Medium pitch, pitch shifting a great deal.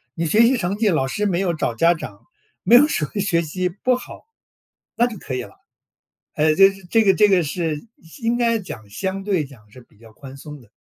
Yes: medium, 180 Hz; wide, 6.0 semitones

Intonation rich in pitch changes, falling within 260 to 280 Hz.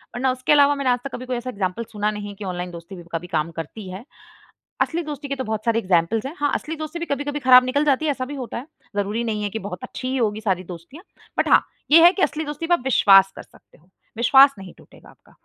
No: wide, 6.4 semitones; high, 240 Hz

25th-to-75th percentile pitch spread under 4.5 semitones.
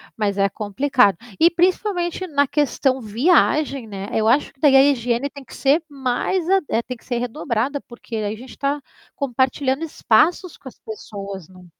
No: average, 4.8 semitones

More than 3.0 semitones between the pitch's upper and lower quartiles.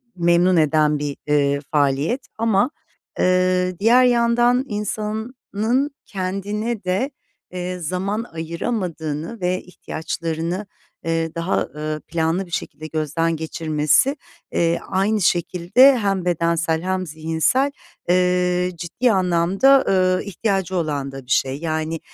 Yes: average, 4.2 semitones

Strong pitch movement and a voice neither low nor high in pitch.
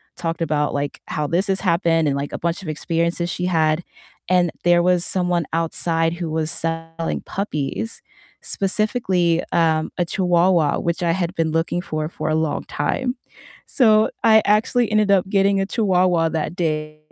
No: average, 2.8 semitones; medium, 170 Hz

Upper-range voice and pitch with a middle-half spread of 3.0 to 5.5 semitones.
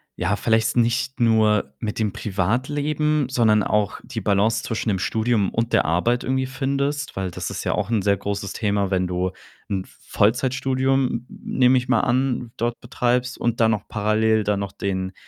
No: low, 110 Hz; average, 3.8 semitones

